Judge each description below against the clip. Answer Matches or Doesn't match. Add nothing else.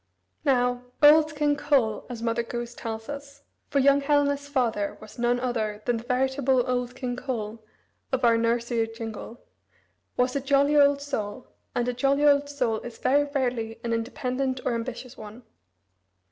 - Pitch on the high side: Matches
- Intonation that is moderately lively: Matches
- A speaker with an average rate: Matches